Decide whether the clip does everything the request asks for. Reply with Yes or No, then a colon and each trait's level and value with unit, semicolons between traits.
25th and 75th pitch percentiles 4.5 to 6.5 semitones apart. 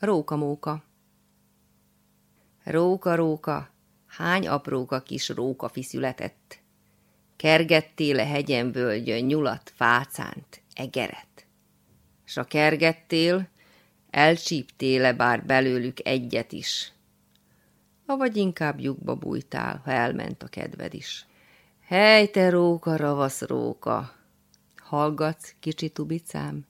Yes: wide, 5.6 semitones